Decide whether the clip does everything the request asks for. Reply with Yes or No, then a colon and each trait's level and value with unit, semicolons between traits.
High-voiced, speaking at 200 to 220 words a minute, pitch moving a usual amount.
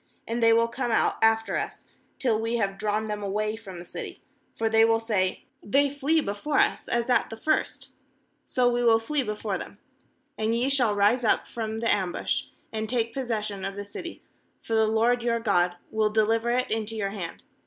No: high, 225 Hz; fast, 205 wpm; narrow, 2.1 semitones